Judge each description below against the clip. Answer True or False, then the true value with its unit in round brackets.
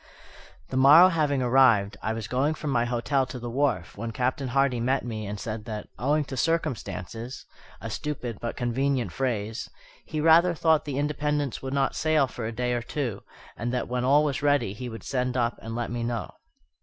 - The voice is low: True (125 Hz)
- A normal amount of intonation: True (3.5 semitones)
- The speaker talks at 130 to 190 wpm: False (200 wpm)